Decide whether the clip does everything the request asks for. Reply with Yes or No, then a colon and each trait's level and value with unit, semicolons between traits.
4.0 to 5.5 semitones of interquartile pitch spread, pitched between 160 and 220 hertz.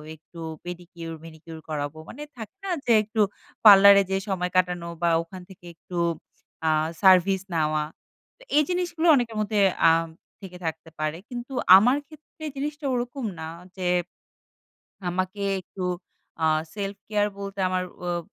Yes: average, 4.6 semitones; high, 190 Hz